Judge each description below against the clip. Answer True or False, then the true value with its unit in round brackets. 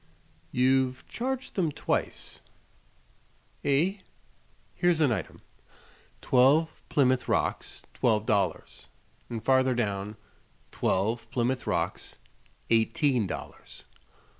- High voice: False (130 Hz)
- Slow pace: True (90 wpm)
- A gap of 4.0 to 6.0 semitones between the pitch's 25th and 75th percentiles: True (4.3 semitones)